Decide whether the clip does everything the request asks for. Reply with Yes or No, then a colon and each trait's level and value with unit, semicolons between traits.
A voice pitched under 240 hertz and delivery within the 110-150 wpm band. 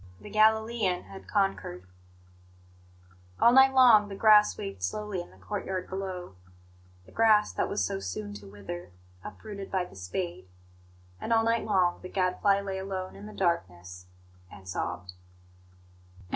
Yes: high, 190 Hz; average, 145 wpm